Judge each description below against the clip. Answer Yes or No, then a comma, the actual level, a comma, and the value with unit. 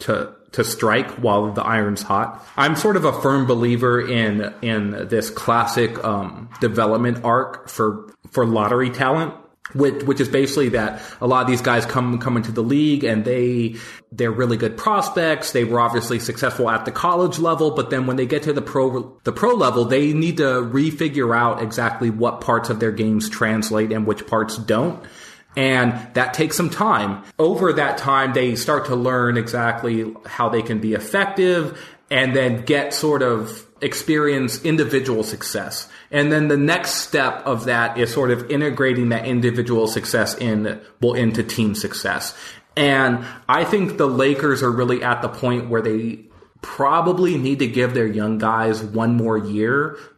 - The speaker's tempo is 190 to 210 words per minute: No, average, 175 wpm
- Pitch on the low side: Yes, low, 125 Hz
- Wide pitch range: No, average, 3.7 semitones